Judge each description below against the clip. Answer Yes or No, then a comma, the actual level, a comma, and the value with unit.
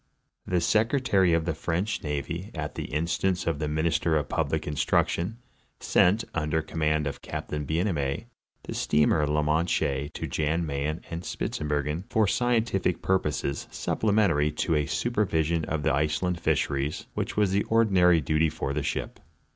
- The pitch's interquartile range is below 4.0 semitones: Yes, average, 3.4 semitones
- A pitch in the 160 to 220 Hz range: No, very low, 80 Hz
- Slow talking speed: No, average, 155 wpm